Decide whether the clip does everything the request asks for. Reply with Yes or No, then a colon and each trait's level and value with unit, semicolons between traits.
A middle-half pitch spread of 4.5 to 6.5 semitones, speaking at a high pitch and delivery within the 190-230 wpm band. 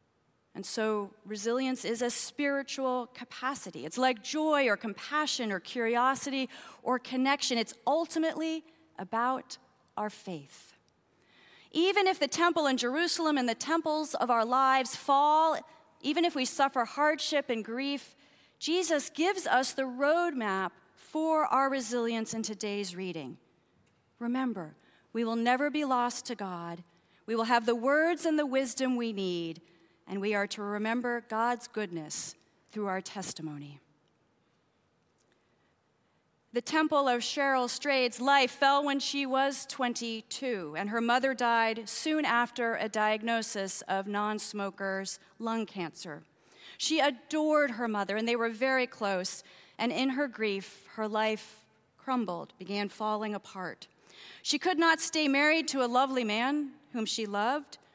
No: average, 4.8 semitones; high, 245 Hz; average, 140 wpm